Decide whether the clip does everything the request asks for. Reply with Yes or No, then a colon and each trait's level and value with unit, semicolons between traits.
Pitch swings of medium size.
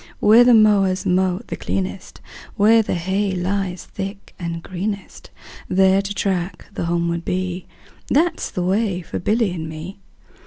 No: narrow, 2.3 semitones